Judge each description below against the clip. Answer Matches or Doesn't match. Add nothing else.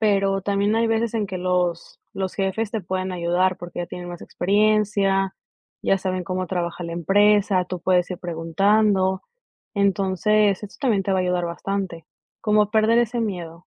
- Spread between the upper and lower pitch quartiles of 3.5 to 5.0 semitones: Doesn't match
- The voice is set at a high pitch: Matches